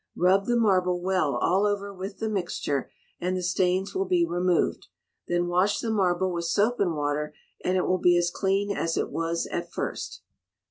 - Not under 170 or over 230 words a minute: Yes, average, 190 wpm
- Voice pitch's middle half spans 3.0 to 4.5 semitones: No, narrow, 2.4 semitones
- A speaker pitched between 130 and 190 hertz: Yes, medium, 185 Hz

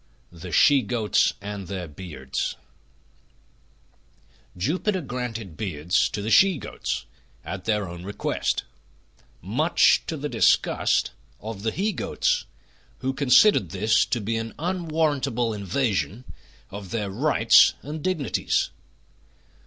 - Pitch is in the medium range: No, low, 110 Hz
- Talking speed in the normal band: No, slow, 115 wpm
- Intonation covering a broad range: Yes, wide, 6.3 semitones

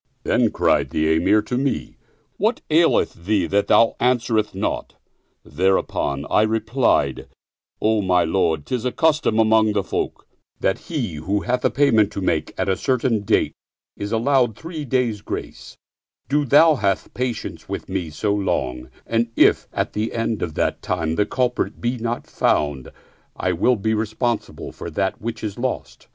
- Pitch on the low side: Yes, low, 110 Hz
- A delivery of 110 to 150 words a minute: No, average, 170 wpm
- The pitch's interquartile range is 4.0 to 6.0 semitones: Yes, average, 4.4 semitones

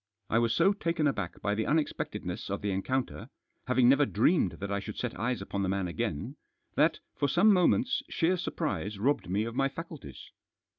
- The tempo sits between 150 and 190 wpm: No, average, 200 wpm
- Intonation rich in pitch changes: Yes, wide, 8.2 semitones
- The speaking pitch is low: Yes, low, 125 Hz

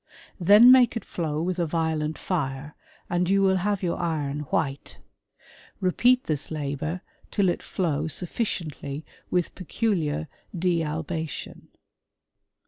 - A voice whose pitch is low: No, medium, 165 Hz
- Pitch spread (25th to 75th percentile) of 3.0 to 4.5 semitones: Yes, average, 3.4 semitones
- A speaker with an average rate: No, slow, 125 wpm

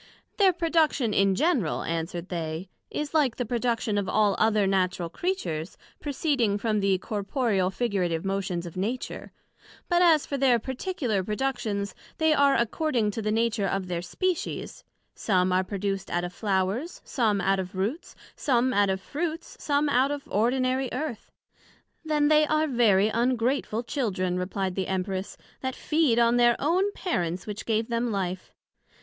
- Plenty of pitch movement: Yes, wide, 6.1 semitones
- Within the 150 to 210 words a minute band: Yes, average, 160 wpm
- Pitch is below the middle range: No, high, 225 Hz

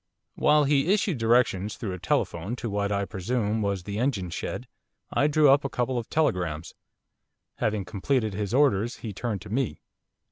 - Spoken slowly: No, average, 175 wpm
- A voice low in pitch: Yes, low, 110 Hz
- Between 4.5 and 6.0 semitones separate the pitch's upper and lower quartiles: Yes, average, 5.2 semitones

